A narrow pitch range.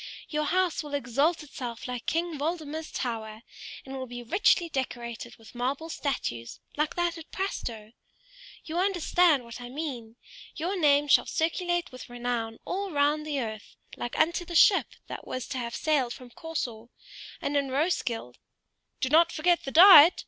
No: average, 5.3 semitones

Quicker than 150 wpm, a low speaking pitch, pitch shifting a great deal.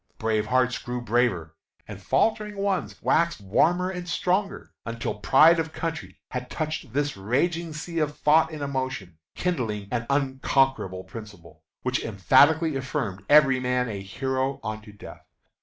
No: average, 140 wpm; low, 130 Hz; wide, 6.4 semitones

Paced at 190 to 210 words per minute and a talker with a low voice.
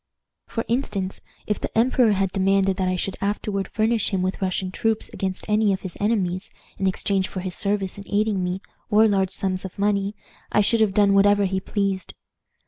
No: average, 195 wpm; high, 195 Hz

